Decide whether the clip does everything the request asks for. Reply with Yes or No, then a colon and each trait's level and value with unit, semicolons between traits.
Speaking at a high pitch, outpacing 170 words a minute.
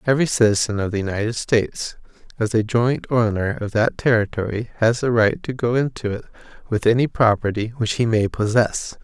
No: low, 115 Hz; average, 180 wpm